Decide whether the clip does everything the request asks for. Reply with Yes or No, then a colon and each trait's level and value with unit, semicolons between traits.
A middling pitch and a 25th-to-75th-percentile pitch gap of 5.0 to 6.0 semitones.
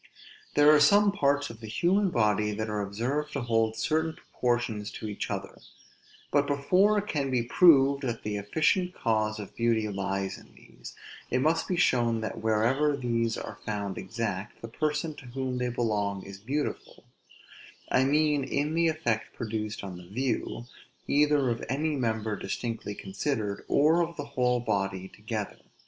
No: low, 120 Hz; wide, 5.4 semitones